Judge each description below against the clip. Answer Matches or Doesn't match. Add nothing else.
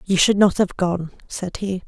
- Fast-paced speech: Matches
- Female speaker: Matches